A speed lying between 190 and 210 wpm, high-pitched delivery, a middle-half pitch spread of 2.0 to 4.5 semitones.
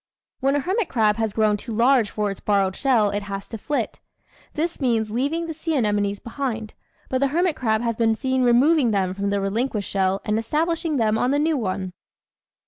No: fast, 205 wpm; high, 230 Hz; average, 5.1 semitones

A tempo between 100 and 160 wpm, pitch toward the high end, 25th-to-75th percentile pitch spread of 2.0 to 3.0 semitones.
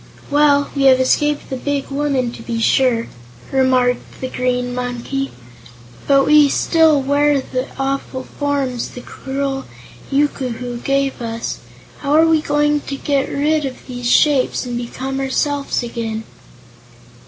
Yes: average, 140 wpm; very high, 270 Hz; narrow, 2.4 semitones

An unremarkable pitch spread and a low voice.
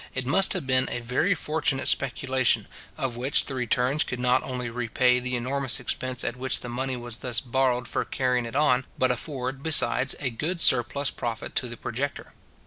No: narrow, 1.6 semitones; low, 130 Hz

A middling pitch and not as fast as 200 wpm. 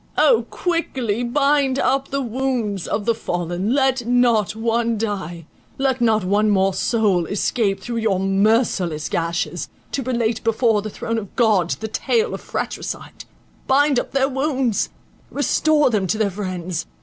No: high, 225 Hz; average, 145 wpm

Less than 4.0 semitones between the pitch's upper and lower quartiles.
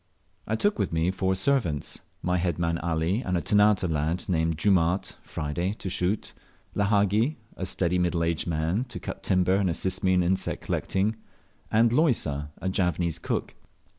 Yes: average, 3.4 semitones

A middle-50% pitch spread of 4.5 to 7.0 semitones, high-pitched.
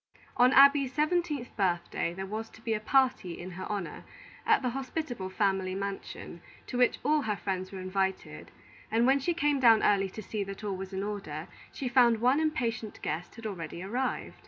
Yes: average, 5.3 semitones; high, 215 Hz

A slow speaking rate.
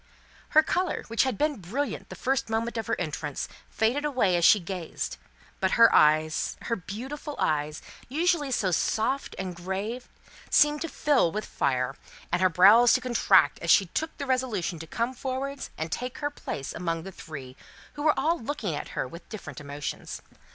No: average, 180 wpm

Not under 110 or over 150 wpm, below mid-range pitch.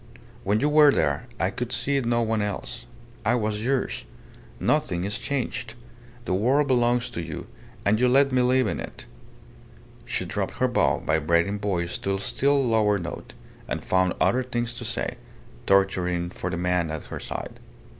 No: average, 175 wpm; low, 110 Hz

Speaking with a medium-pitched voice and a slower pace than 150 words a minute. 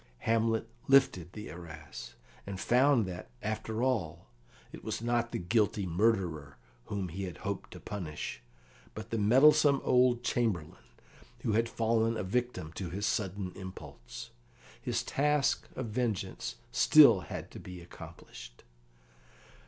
No: low, 105 Hz; slow, 135 wpm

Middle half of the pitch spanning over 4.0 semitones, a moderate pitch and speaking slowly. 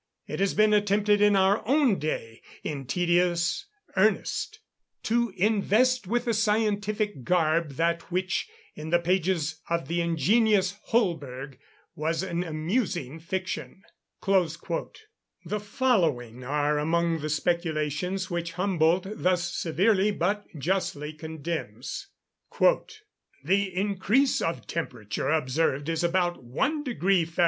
Yes: average, 4.6 semitones; medium, 175 Hz; slow, 115 wpm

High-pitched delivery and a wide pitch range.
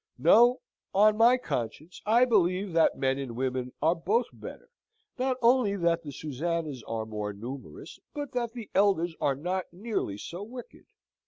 No: medium, 175 Hz; wide, 8.8 semitones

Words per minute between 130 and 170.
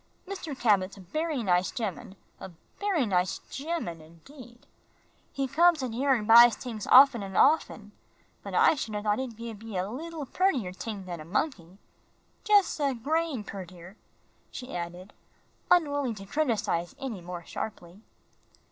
Yes: average, 155 wpm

